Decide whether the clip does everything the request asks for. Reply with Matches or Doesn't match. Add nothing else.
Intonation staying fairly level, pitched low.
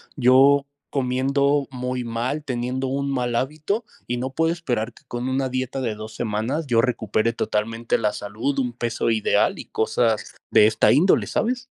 Doesn't match